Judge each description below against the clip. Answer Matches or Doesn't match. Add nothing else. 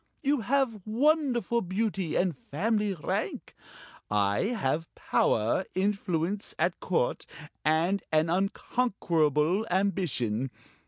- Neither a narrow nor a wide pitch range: Doesn't match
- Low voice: Doesn't match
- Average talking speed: Doesn't match